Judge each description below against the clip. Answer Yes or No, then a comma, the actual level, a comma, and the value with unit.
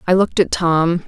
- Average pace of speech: No, fast, 225 wpm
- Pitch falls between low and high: Yes, medium, 175 Hz